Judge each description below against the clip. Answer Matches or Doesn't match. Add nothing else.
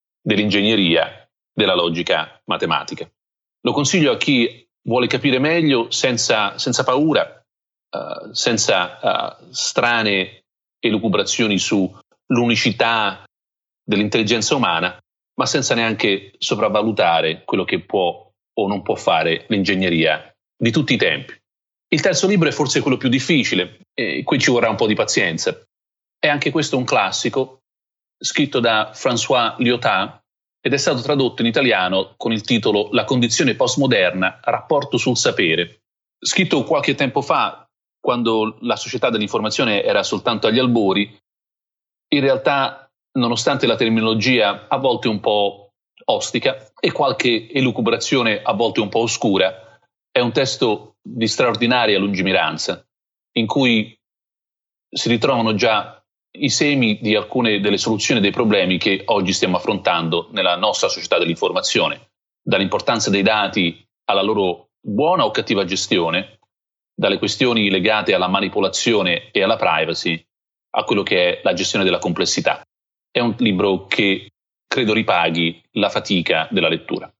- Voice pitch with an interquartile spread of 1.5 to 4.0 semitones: Doesn't match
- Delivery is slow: Doesn't match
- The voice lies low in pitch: Matches